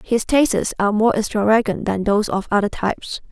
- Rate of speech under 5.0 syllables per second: No, 6.3 syllables/s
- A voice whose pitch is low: No, high, 210 Hz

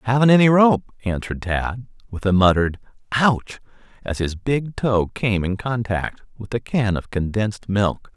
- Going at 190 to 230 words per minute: No, average, 160 wpm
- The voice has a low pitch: Yes, low, 110 Hz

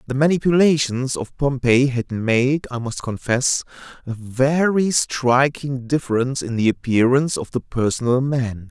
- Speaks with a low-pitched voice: Yes, low, 130 Hz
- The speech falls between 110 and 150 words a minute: Yes, average, 140 wpm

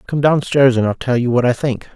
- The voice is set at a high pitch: No, low, 130 Hz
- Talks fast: Yes, fast, 305 wpm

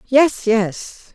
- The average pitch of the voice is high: Yes, high, 235 Hz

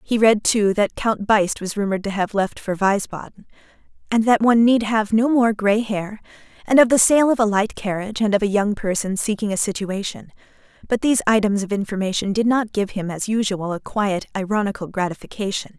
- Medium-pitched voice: No, high, 210 Hz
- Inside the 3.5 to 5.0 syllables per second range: No, 5.6 syllables/s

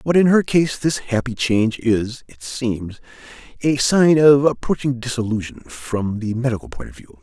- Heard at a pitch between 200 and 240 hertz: No, low, 125 Hz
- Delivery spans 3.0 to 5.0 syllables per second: Yes, 4.6 syllables/s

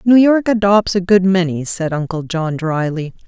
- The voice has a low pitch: No, medium, 185 Hz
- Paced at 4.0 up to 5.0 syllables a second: Yes, 4.6 syllables/s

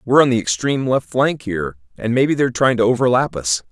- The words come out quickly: Yes, fast, 225 wpm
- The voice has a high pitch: No, low, 120 Hz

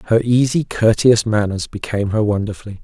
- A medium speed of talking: Yes, average, 150 wpm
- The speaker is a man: Yes, male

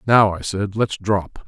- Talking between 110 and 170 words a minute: No, fast, 205 wpm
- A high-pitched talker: No, low, 100 Hz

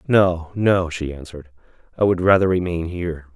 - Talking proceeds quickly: No, average, 160 wpm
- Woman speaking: No, male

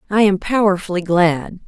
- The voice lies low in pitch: No, high, 190 Hz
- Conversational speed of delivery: Yes, average, 145 wpm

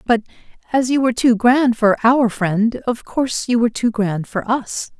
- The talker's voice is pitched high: Yes, high, 235 Hz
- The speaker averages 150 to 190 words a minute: No, fast, 205 wpm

